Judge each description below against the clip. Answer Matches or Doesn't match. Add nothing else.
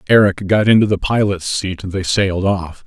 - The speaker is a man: Matches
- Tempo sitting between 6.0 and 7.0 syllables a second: Doesn't match